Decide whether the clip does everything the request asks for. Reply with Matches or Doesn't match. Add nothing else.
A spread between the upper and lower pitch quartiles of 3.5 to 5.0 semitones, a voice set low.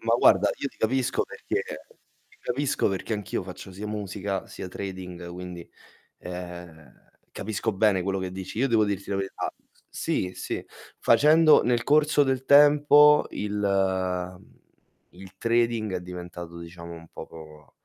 Matches